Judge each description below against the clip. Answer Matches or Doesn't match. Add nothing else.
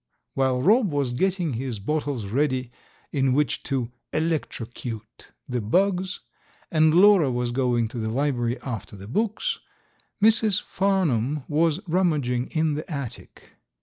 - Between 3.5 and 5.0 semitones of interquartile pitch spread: Doesn't match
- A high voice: Doesn't match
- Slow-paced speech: Matches